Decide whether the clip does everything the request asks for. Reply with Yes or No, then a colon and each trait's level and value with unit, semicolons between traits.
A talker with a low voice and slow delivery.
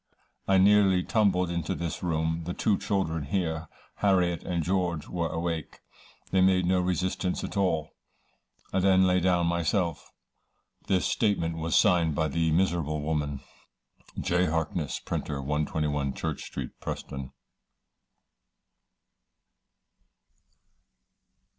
Yes: very low, 85 Hz; slow, 115 wpm